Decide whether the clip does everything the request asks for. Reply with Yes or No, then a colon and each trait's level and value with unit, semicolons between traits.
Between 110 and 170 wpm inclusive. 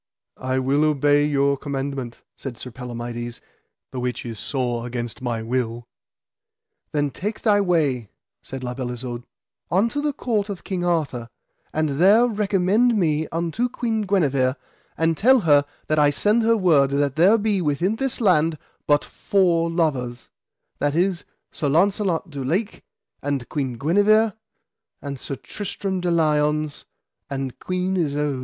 Yes: average, 150 wpm